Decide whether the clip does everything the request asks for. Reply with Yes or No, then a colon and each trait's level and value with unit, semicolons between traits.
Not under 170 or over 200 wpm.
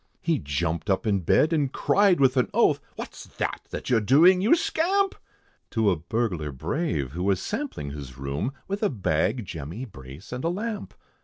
Yes: average, 185 wpm